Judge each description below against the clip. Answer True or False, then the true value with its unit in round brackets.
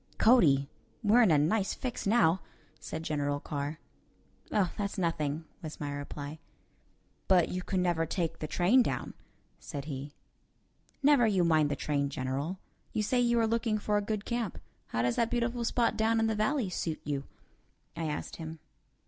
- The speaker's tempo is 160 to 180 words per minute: True (175 wpm)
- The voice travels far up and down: True (6.9 semitones)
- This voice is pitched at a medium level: True (175 Hz)